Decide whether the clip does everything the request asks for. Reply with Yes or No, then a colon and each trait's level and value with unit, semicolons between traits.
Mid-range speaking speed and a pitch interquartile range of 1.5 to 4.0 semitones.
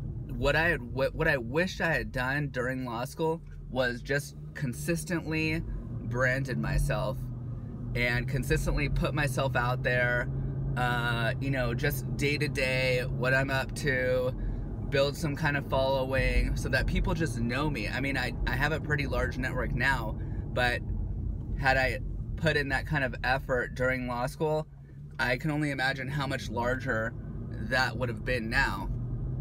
Yes: average, 155 wpm; narrow, 2.4 semitones